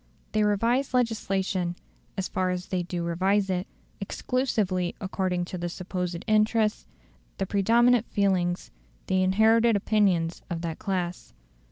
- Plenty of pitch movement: No, average, 3.2 semitones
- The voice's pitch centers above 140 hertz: Yes, high, 190 Hz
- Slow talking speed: Yes, slow, 130 wpm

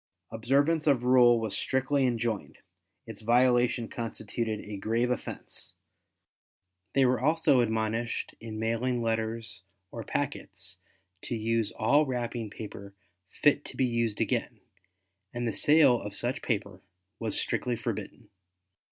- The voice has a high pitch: No, low, 115 Hz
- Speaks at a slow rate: Yes, slow, 125 wpm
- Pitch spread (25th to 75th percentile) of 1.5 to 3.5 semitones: Yes, narrow, 2.5 semitones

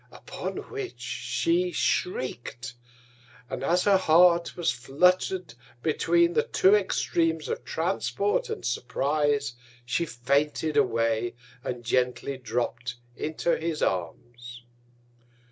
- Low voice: No, medium, 150 Hz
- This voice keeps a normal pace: No, slow, 105 wpm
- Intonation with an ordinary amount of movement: No, wide, 6.2 semitones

